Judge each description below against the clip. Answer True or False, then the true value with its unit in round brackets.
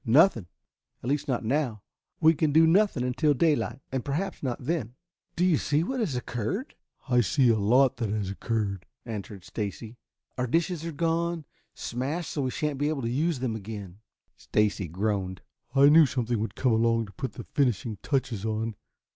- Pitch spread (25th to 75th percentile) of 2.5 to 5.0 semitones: False (5.5 semitones)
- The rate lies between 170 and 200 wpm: True (180 wpm)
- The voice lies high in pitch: False (125 Hz)